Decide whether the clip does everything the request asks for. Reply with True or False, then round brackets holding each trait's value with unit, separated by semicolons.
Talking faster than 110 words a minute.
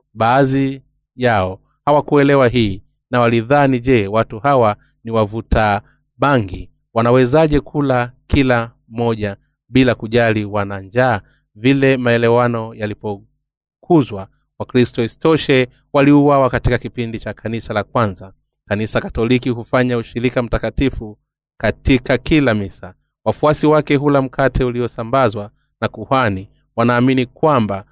False (105 wpm)